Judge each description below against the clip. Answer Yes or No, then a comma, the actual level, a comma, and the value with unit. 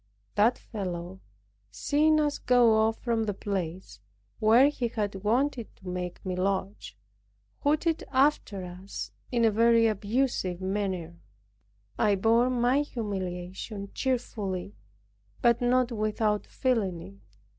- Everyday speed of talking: No, slow, 120 wpm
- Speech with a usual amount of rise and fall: Yes, average, 4.5 semitones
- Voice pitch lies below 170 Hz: No, high, 215 Hz